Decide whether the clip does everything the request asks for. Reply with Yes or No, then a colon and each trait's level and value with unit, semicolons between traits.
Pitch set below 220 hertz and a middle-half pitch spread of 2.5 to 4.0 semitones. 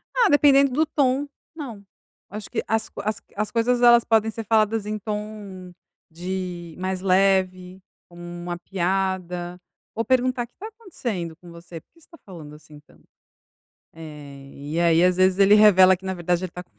No: high, 190 Hz; average, 4.4 semitones